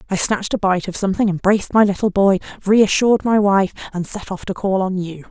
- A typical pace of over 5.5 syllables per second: Yes, 6.1 syllables/s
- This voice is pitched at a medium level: No, high, 195 Hz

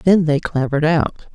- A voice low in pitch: No, medium, 155 Hz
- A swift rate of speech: No, average, 180 wpm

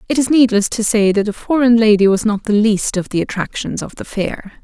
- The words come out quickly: Yes, fast, 245 wpm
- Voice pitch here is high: Yes, high, 215 Hz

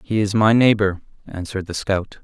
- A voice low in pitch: Yes, low, 100 Hz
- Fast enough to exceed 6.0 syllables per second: No, 5.3 syllables/s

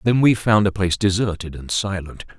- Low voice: Yes, low, 100 Hz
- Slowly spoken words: No, average, 200 wpm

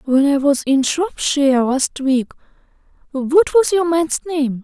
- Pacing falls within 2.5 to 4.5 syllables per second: Yes, 4.0 syllables/s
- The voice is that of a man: No, female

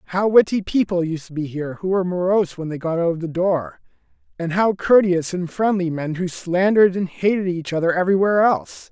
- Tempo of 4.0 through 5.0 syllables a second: No, 5.9 syllables/s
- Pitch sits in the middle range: Yes, medium, 180 Hz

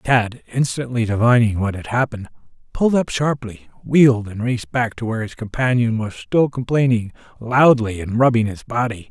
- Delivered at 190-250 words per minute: No, average, 165 wpm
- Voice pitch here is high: No, low, 120 Hz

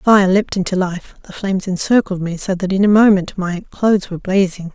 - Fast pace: Yes, fast, 225 wpm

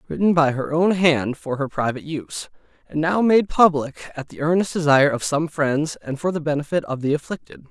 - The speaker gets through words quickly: Yes, fast, 210 wpm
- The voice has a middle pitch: Yes, medium, 155 Hz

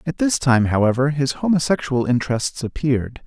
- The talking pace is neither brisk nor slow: Yes, average, 145 wpm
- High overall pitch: No, low, 135 Hz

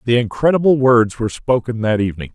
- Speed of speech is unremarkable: Yes, average, 180 wpm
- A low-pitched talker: Yes, low, 120 Hz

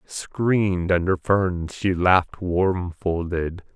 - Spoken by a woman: No, male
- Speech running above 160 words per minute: No, slow, 95 wpm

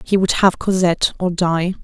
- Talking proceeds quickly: No, average, 195 wpm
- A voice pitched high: No, medium, 180 Hz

